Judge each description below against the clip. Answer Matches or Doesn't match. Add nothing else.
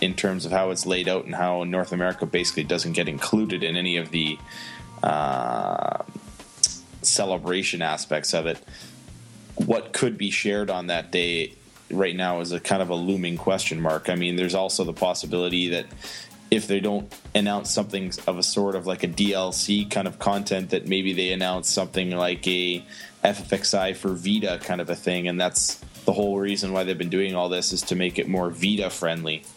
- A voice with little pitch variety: Matches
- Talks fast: Doesn't match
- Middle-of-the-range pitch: Doesn't match